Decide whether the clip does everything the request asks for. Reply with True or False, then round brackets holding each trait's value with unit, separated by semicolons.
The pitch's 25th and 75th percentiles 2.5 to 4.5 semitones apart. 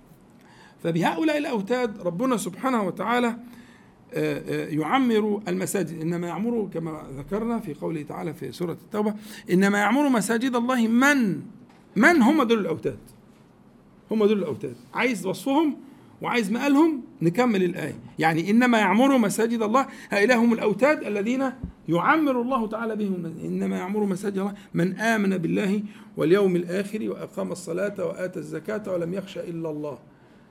False (5.3 semitones)